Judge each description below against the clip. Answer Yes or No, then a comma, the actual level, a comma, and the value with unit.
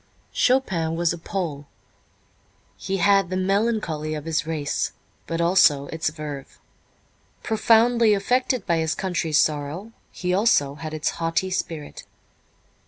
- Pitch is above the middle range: No, medium, 170 Hz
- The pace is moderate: No, slow, 125 wpm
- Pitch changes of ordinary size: Yes, average, 4.3 semitones